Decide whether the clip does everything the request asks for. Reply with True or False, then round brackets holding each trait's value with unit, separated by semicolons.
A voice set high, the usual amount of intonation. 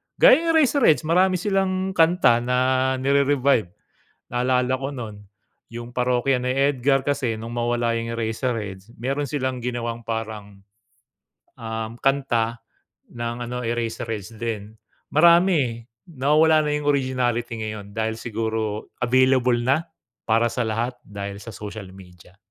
False (120 Hz; 3.6 semitones)